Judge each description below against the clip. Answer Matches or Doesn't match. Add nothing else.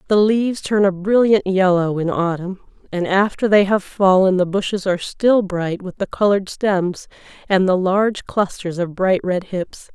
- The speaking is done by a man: Doesn't match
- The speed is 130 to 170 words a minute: Doesn't match